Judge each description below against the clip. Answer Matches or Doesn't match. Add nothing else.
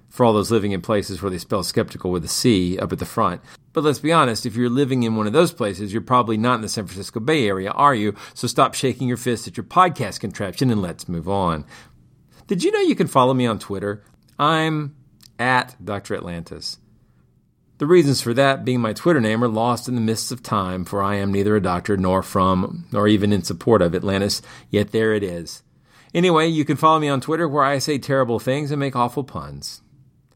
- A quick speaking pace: Matches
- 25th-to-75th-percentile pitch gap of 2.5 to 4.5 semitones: Doesn't match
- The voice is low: Matches